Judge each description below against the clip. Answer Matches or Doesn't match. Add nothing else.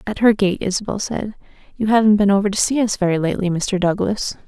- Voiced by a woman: Matches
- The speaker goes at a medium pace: Doesn't match